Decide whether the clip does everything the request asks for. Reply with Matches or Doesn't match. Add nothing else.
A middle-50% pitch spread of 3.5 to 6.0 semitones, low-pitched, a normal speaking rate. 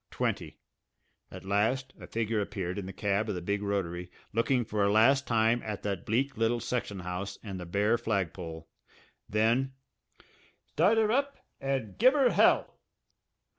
Matches